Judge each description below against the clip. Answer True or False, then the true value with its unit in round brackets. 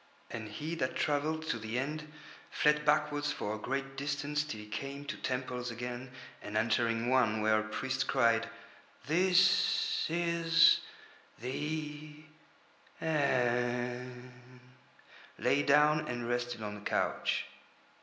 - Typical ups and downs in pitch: True (3.7 semitones)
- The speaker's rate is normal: False (125 wpm)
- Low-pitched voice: True (130 Hz)